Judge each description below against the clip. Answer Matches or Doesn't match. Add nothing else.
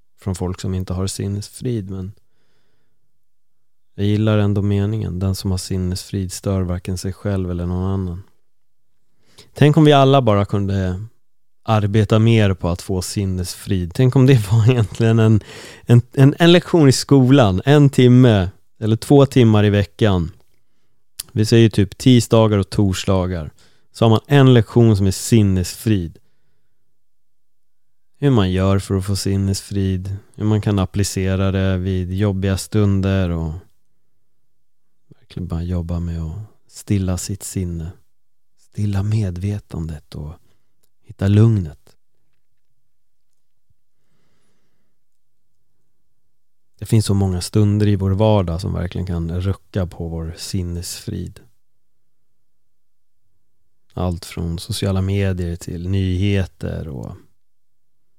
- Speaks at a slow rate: Matches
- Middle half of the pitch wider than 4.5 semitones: Doesn't match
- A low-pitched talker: Matches